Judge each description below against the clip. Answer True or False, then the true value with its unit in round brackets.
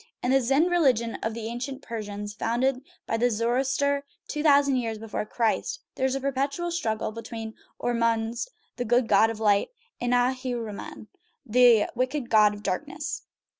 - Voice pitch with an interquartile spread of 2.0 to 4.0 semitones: True (3.3 semitones)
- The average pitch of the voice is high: True (245 Hz)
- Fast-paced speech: False (155 wpm)